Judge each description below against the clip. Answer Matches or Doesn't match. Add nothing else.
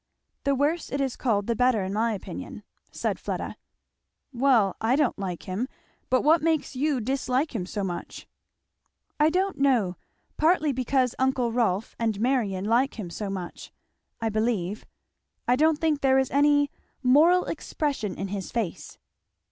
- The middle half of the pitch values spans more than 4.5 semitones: Matches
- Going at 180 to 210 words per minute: Doesn't match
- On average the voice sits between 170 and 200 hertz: Doesn't match